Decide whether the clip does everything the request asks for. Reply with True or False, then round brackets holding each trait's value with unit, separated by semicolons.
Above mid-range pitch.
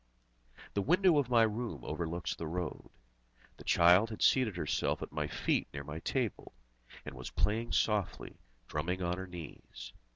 False (90 Hz)